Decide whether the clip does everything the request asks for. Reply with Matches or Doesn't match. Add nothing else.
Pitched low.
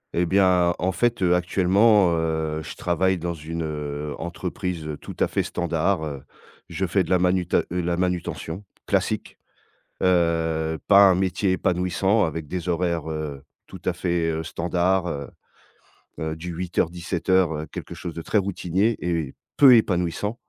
Matches